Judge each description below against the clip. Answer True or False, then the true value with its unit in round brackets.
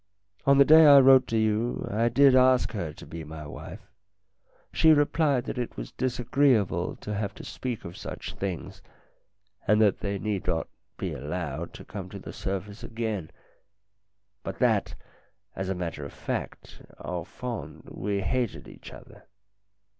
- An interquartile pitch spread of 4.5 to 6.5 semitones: True (5.3 semitones)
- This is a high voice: False (105 Hz)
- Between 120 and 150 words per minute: False (160 wpm)